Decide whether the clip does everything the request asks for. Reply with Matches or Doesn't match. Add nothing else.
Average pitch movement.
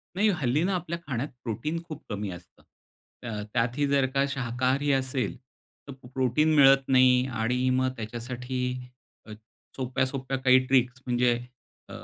Doesn't match